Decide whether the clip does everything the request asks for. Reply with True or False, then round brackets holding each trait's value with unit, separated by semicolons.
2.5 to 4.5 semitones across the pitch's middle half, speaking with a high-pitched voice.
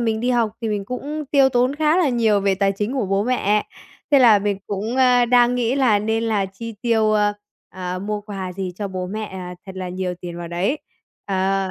True (4.0 semitones; 210 Hz)